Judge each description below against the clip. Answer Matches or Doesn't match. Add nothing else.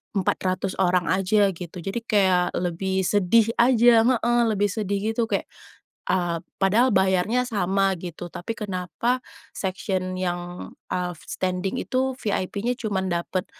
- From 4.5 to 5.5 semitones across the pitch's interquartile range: Doesn't match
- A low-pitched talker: Doesn't match